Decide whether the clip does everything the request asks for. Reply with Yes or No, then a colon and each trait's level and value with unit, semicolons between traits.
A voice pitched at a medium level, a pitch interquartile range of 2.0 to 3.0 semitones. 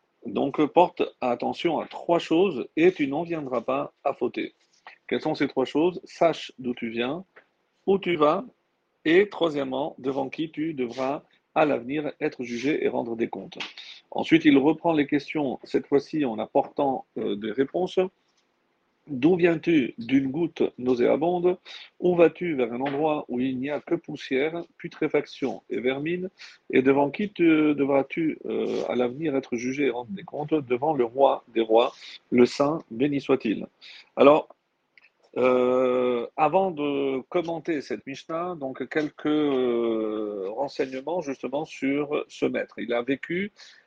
No: medium, 150 Hz; average, 5.2 semitones